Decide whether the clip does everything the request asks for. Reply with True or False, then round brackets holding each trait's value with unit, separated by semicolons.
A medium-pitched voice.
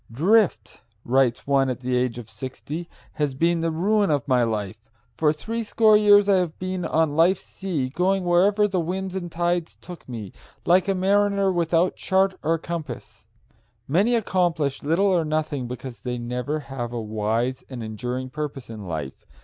True (155 Hz)